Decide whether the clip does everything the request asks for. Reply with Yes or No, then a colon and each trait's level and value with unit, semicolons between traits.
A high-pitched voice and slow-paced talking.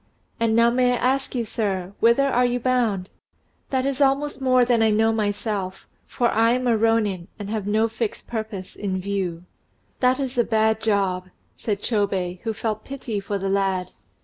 No: high, 220 Hz; average, 185 wpm